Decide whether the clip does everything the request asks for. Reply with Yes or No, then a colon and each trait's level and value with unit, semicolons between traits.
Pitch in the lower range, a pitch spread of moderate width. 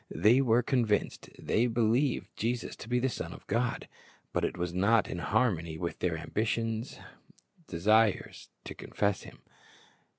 Yes: low, 110 Hz; average, 4.1 semitones